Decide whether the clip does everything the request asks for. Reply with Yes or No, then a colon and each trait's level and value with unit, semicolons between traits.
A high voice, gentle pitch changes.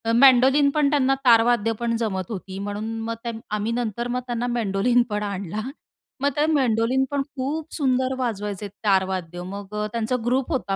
No: high, 230 Hz; average, 4.1 semitones